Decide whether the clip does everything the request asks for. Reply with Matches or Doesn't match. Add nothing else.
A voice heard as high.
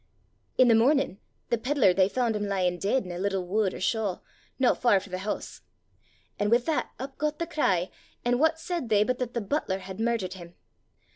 Matches